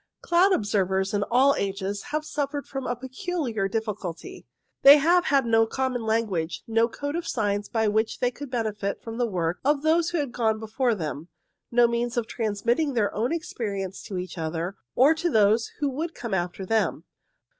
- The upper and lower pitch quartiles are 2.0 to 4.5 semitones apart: No, wide, 5.4 semitones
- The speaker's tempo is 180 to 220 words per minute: Yes, average, 185 wpm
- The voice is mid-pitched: No, high, 230 Hz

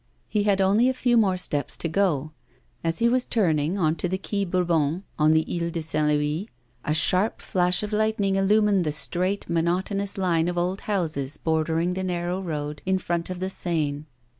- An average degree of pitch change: Yes, average, 3.6 semitones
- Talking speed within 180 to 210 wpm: Yes, average, 190 wpm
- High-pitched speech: No, medium, 180 Hz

